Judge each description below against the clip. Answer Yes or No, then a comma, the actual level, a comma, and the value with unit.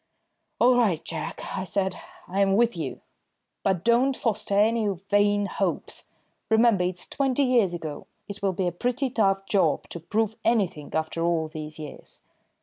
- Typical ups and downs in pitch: Yes, average, 4.7 semitones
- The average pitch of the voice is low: No, high, 200 Hz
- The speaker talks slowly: No, average, 155 wpm